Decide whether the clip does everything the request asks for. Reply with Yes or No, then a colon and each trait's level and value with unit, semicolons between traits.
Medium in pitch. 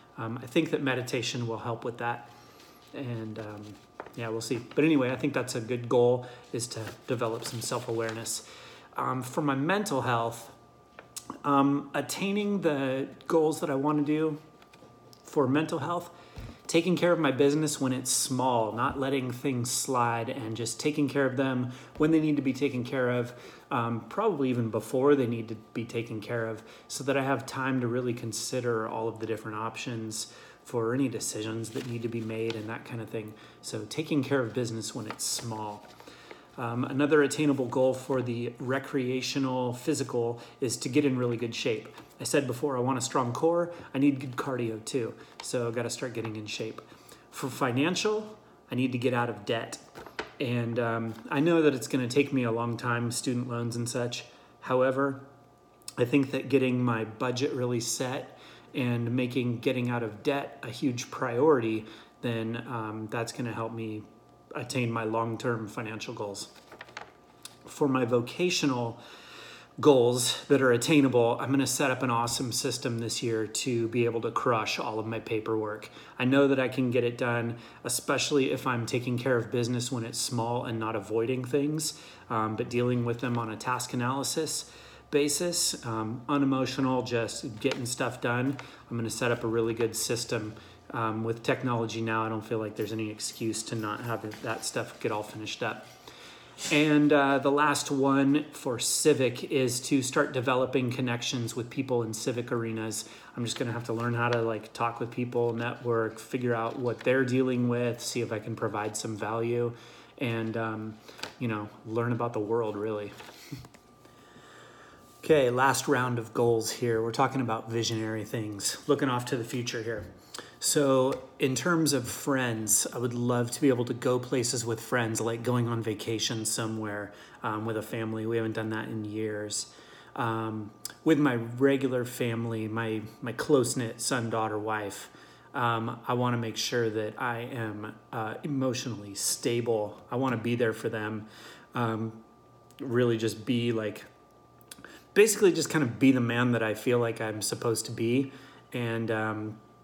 No: low, 120 Hz